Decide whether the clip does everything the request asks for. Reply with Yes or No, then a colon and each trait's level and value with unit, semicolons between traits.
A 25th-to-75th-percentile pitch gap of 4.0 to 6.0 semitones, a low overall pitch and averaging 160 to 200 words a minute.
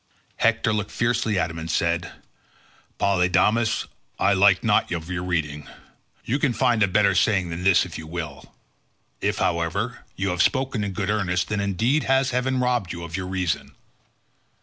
Yes: average, 5.0 semitones; very low, 95 Hz; average, 170 wpm